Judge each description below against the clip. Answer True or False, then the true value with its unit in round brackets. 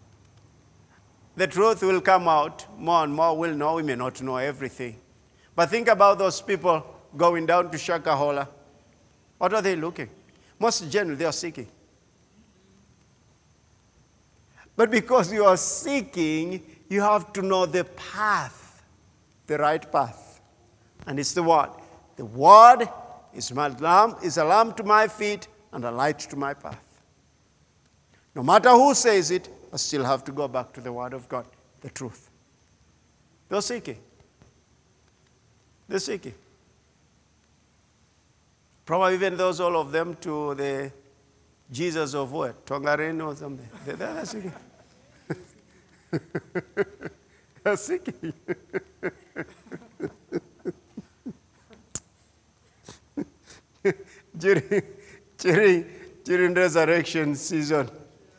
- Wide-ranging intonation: True (6.1 semitones)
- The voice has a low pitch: False (160 Hz)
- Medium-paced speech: False (115 wpm)